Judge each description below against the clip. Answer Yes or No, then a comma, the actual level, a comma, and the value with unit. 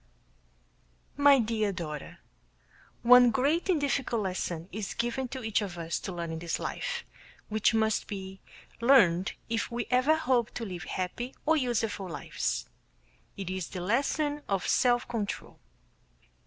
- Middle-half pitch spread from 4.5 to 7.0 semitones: Yes, wide, 5.4 semitones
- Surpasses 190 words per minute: No, average, 145 wpm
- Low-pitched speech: No, high, 225 Hz